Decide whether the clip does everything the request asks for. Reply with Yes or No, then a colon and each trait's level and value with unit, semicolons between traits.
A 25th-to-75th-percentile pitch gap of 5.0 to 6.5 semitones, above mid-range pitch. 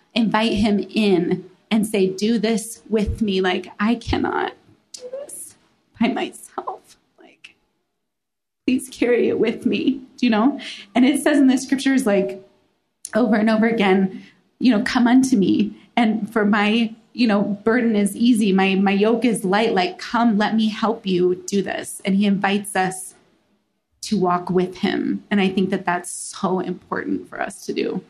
No: average, 3.2 semitones; high, 215 Hz